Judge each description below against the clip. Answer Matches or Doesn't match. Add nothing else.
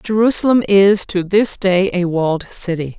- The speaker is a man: Doesn't match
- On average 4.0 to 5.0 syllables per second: Matches